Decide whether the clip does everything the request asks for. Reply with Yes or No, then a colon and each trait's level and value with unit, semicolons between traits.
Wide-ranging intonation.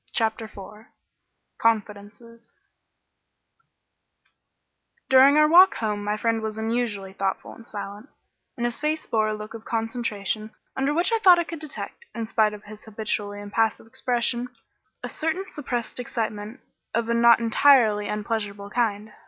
No: average, 2.8 semitones